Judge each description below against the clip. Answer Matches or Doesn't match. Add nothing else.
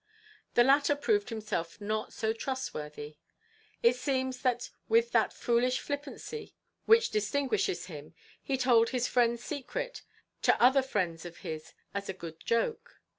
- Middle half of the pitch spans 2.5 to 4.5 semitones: Doesn't match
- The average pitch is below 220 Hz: Doesn't match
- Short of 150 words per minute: Matches